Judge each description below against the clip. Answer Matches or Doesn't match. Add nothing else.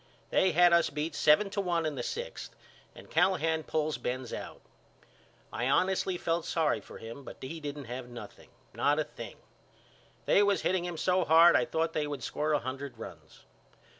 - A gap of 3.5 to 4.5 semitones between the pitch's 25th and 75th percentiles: Matches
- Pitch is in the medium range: Matches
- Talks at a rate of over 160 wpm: Matches